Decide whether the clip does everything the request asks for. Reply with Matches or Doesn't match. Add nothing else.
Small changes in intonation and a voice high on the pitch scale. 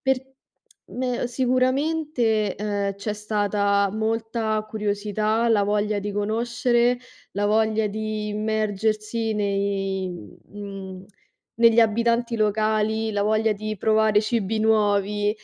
Matches